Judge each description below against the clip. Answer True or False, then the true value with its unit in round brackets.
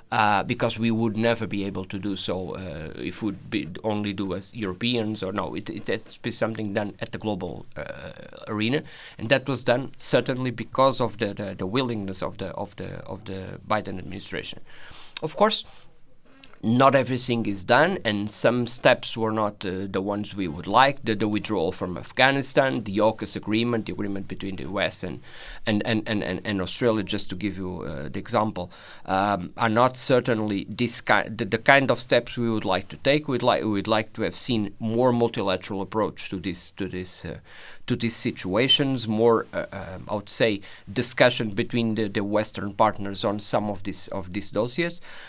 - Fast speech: False (195 wpm)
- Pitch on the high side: False (110 Hz)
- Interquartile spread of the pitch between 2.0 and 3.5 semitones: True (3.2 semitones)